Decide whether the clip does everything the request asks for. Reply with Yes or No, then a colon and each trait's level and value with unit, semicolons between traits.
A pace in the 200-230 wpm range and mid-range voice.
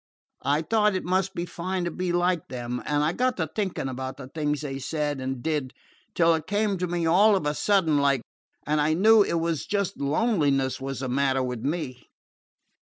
Yes: fast, 205 wpm; medium, 155 Hz